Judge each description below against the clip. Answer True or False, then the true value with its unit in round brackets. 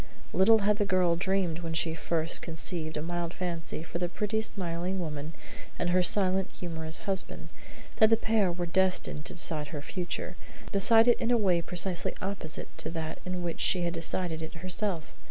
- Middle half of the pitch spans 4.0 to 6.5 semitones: False (2.7 semitones)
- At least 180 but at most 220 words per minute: True (185 wpm)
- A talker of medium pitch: True (175 Hz)